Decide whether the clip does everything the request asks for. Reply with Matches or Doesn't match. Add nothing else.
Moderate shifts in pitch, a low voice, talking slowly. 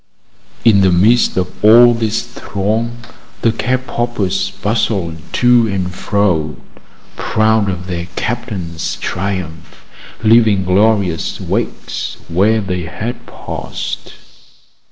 Matches